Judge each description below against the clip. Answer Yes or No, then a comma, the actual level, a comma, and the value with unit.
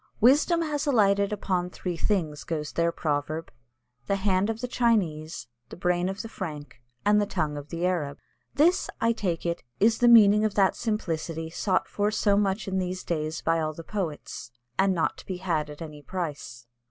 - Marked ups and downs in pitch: No, average, 4.7 semitones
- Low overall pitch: No, medium, 185 Hz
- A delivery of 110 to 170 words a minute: No, average, 190 wpm